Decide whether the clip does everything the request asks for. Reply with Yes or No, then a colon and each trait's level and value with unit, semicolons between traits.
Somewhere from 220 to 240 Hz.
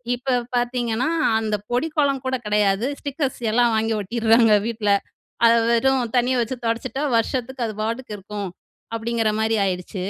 Yes: high, 230 Hz